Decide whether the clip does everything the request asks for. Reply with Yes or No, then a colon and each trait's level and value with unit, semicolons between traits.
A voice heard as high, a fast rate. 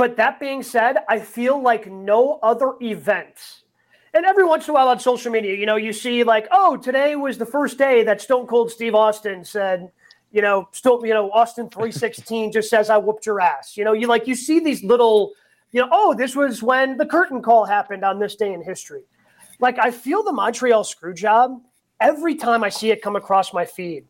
Yes: high, 230 Hz; fast, 220 wpm